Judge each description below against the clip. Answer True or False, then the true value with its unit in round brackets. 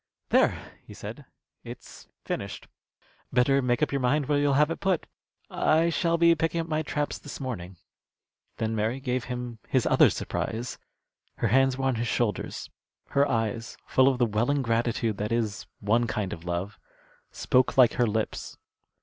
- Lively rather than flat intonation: False (4.1 semitones)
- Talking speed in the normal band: True (170 wpm)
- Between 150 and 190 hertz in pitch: False (125 Hz)